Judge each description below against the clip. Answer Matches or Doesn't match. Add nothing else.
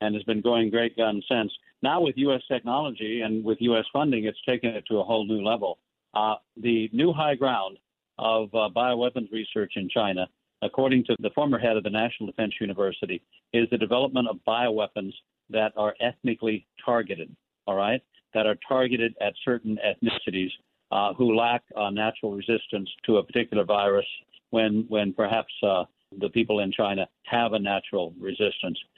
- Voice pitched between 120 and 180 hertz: Doesn't match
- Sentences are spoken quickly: Doesn't match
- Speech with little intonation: Matches